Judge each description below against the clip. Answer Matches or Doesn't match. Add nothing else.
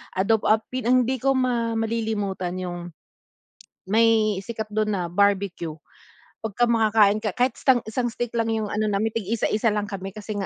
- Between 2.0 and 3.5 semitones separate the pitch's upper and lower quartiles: Matches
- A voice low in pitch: Doesn't match